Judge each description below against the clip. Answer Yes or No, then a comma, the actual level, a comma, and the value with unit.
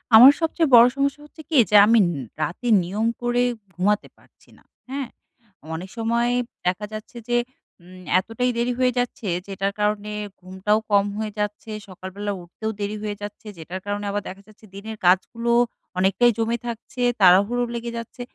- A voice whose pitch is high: Yes, high, 215 Hz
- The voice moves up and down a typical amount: Yes, average, 3.3 semitones